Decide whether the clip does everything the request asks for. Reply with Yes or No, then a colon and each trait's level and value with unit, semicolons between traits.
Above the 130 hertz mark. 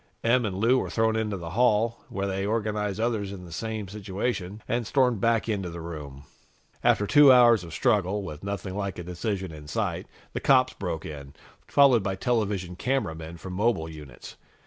No: low, 100 Hz